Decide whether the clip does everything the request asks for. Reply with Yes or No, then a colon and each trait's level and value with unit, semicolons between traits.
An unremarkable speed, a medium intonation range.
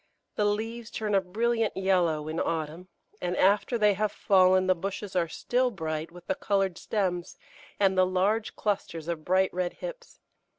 Yes: average, 170 wpm; average, 3.0 semitones